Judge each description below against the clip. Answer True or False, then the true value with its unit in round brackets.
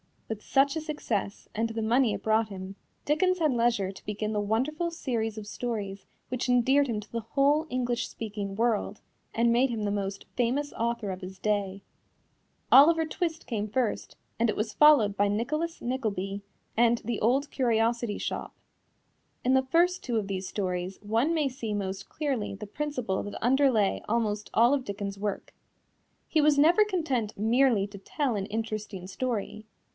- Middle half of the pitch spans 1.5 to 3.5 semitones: False (4.6 semitones)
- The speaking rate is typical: True (170 wpm)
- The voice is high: True (230 Hz)